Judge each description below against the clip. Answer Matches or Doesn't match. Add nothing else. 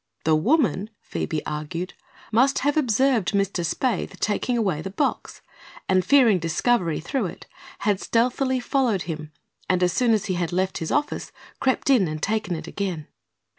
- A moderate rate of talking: Matches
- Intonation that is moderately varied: Doesn't match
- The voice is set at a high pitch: Matches